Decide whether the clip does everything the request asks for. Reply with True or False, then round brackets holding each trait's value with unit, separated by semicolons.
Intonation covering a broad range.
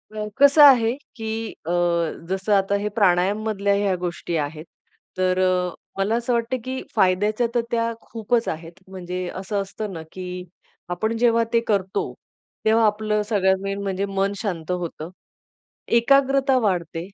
False (3.7 semitones)